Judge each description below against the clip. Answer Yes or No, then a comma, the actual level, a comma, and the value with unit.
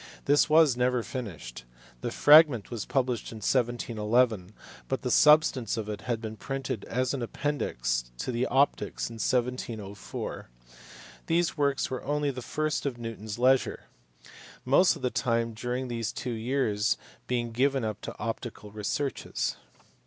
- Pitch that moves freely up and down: No, average, 3.3 semitones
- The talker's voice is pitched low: Yes, low, 120 Hz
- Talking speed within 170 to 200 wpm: No, average, 150 wpm